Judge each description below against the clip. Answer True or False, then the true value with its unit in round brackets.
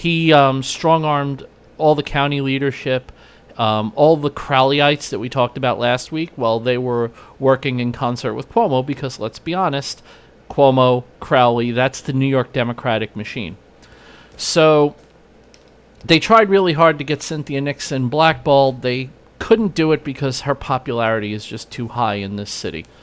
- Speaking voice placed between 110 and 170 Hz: True (135 Hz)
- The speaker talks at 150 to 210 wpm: True (165 wpm)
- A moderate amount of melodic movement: True (3.4 semitones)